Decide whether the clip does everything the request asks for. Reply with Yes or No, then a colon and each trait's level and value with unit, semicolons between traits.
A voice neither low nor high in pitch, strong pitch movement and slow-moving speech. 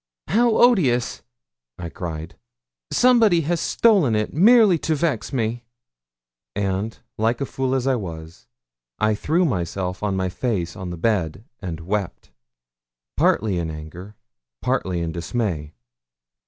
No: low, 105 Hz; wide, 7.9 semitones; slow, 130 wpm